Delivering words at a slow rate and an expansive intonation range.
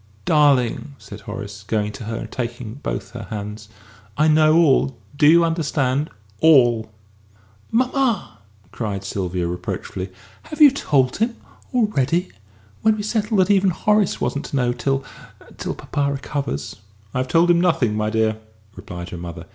No: average, 155 wpm; wide, 7.9 semitones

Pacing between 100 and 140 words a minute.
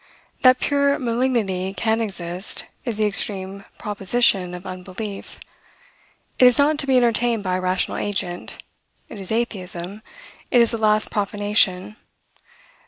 Yes: slow, 135 wpm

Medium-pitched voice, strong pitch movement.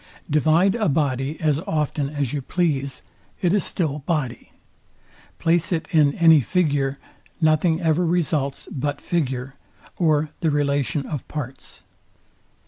No: medium, 150 Hz; average, 2.8 semitones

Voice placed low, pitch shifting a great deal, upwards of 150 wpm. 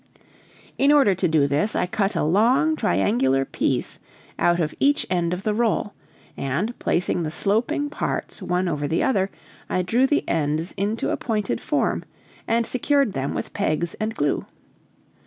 No: medium, 185 Hz; wide, 6.5 semitones; average, 165 wpm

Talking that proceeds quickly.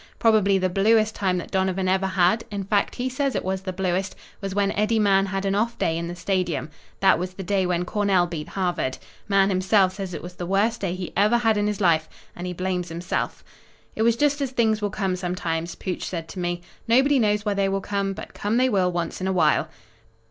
Yes: fast, 235 wpm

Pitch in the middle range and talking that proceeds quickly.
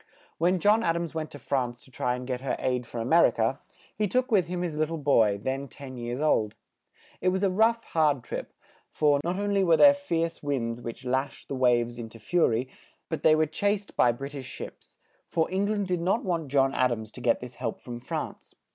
Yes: medium, 145 Hz; fast, 240 wpm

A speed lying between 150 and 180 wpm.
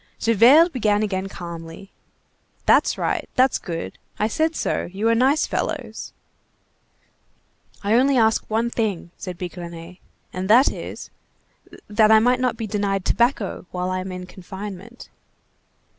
No: average, 140 wpm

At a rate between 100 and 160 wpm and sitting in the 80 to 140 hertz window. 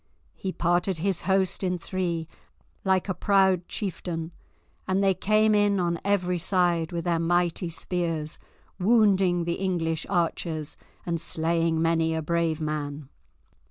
No: slow, 135 wpm; medium, 175 Hz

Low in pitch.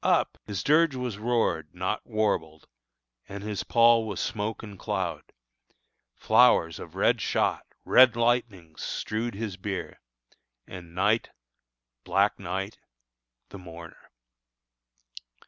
Yes: low, 105 Hz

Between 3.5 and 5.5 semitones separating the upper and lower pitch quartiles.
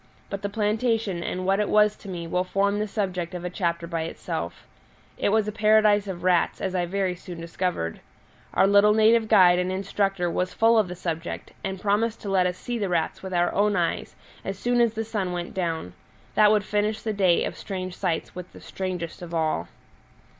No: average, 3.0 semitones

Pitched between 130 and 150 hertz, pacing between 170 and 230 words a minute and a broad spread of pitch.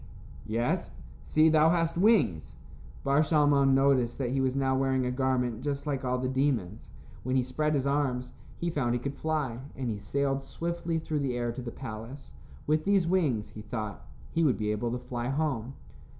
No: low, 135 Hz; average, 195 wpm; average, 3.6 semitones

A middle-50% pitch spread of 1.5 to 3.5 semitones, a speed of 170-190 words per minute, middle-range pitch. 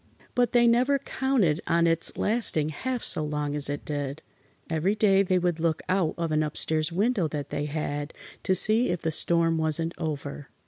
No: average, 4.5 semitones; average, 185 wpm; medium, 165 Hz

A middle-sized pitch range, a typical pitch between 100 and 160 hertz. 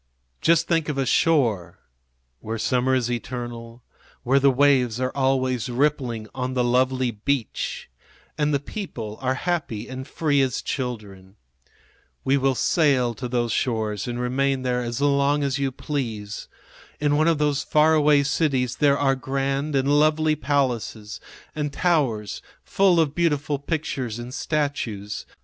Yes: average, 3.3 semitones; low, 135 Hz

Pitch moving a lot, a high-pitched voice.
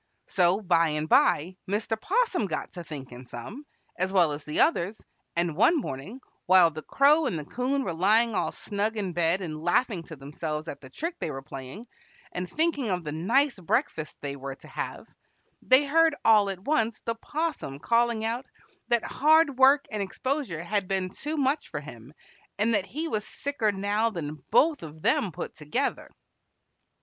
Yes: wide, 8.2 semitones; high, 200 Hz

